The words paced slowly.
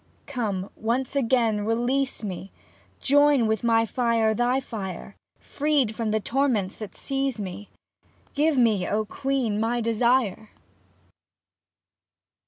Yes: slow, 120 wpm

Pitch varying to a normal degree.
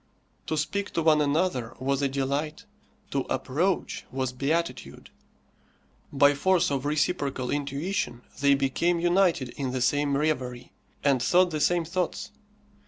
Yes: average, 3.9 semitones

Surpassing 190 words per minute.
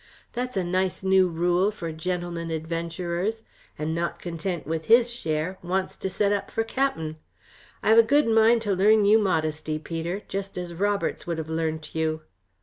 No: average, 175 wpm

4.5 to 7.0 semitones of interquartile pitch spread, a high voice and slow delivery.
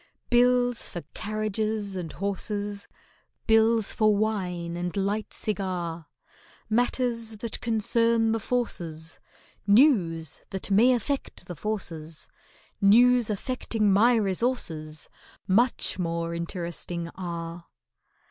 Yes: average, 4.9 semitones; high, 205 Hz; slow, 100 wpm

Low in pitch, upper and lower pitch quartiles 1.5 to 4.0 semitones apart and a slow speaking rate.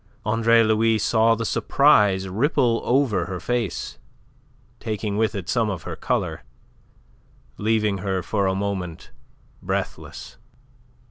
Yes: low, 110 Hz; average, 2.9 semitones; slow, 120 wpm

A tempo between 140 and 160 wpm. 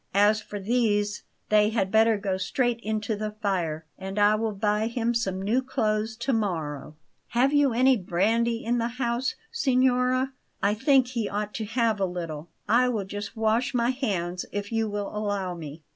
No: average, 180 wpm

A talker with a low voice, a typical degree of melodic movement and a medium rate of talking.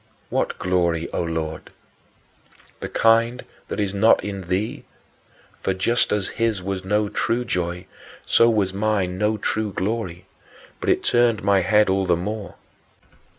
Yes: low, 100 Hz; average, 3.1 semitones; average, 150 wpm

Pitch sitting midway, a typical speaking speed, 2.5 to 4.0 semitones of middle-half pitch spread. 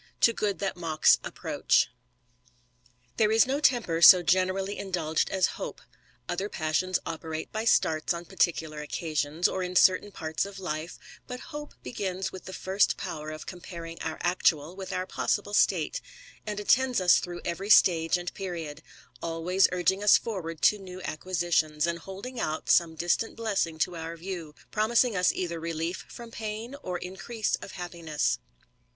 Yes: medium, 180 Hz; average, 160 wpm; average, 3.4 semitones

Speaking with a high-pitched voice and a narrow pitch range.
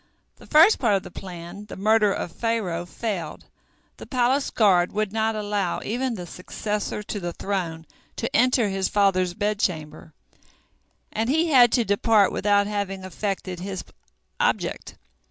No: high, 205 Hz; average, 3.3 semitones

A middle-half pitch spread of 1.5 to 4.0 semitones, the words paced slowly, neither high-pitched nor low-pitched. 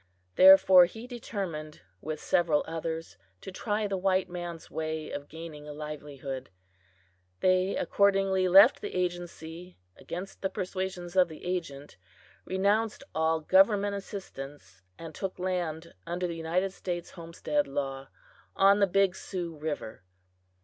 Yes: average, 3.3 semitones; slow, 130 wpm; medium, 175 Hz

